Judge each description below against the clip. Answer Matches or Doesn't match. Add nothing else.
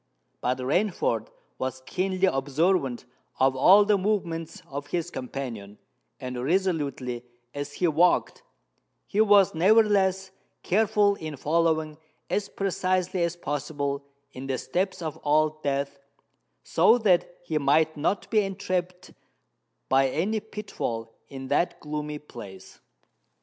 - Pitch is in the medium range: Matches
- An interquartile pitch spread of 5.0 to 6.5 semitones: Matches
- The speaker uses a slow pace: Matches